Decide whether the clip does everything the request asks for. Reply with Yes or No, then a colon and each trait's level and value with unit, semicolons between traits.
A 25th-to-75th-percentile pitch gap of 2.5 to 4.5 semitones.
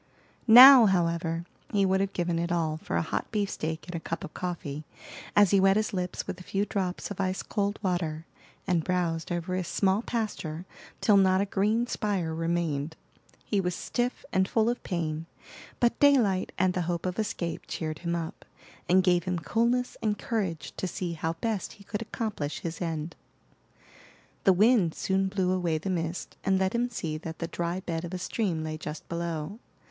Yes: average, 3.3 semitones